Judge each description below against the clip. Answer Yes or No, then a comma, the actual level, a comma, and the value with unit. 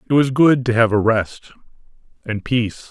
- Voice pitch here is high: No, low, 120 Hz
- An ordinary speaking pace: Yes, average, 165 wpm